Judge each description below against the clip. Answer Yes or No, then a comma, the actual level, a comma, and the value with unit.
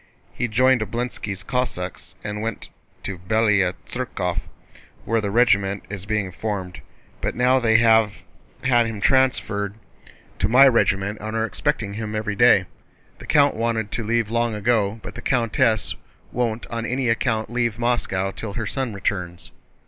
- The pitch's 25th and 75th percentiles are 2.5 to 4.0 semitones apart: Yes, average, 2.9 semitones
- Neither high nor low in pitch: No, low, 110 Hz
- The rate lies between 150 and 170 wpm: Yes, average, 155 wpm